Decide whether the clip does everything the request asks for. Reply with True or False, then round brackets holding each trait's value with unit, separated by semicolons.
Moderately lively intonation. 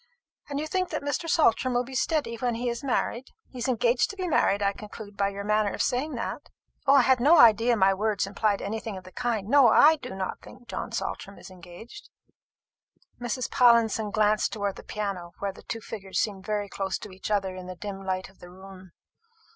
True (4.0 semitones)